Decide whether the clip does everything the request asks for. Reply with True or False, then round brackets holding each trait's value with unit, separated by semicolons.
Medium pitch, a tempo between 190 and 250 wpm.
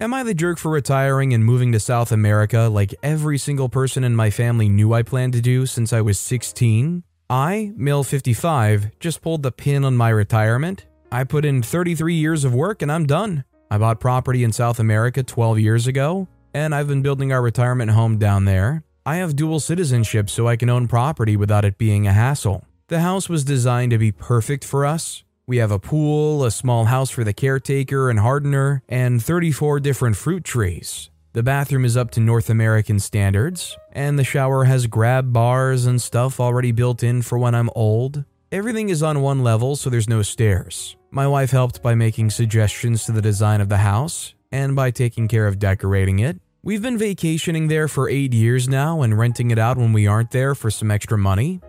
False (125 Hz; 205 wpm)